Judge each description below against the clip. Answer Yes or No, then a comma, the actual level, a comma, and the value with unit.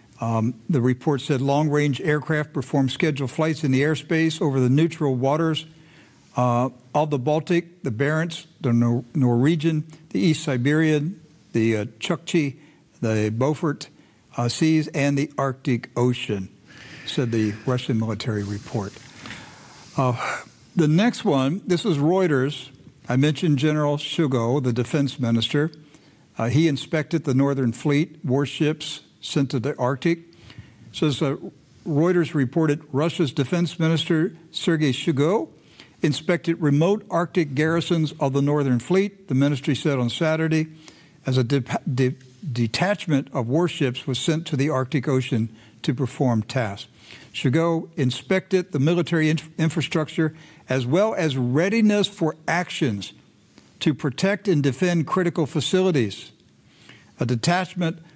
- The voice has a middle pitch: Yes, medium, 150 Hz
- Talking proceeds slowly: Yes, slow, 130 wpm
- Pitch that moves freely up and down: No, average, 3.9 semitones